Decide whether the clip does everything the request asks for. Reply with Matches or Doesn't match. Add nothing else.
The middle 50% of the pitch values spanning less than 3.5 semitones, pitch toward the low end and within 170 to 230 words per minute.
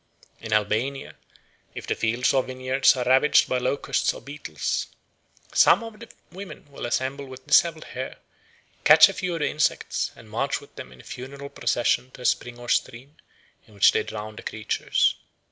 Matches